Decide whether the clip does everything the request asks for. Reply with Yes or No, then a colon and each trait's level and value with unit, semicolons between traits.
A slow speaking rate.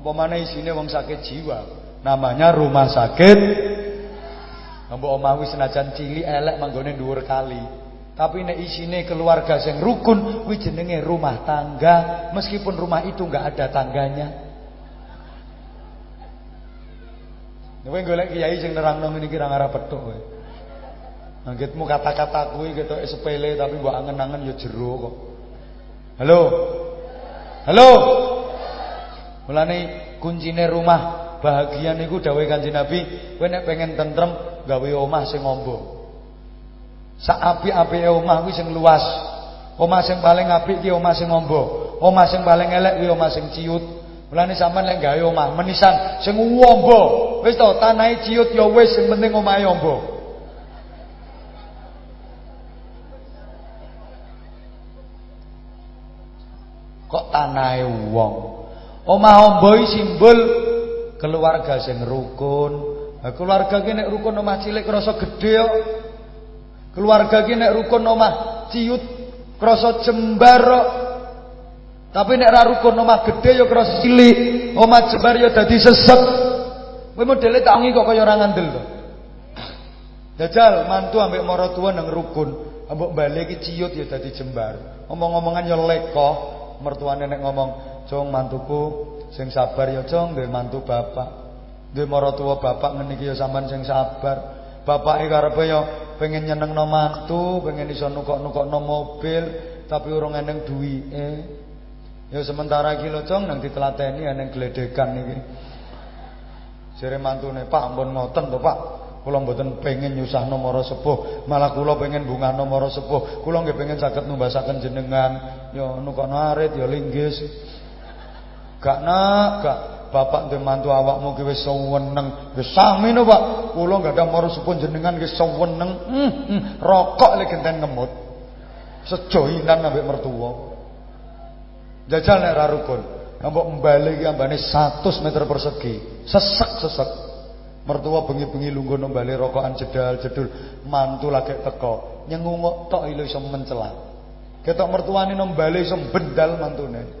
Yes: slow, 130 wpm